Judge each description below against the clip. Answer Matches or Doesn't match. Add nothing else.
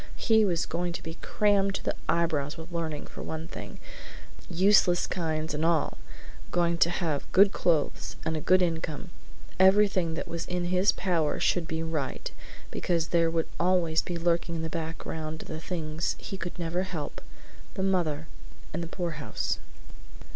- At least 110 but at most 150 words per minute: Doesn't match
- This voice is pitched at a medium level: Matches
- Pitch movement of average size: Doesn't match